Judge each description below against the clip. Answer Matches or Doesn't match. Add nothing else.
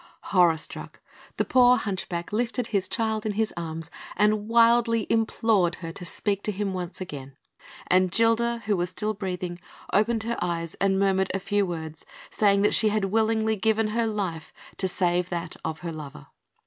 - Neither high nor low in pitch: Doesn't match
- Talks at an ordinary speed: Matches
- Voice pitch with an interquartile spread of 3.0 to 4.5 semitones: Matches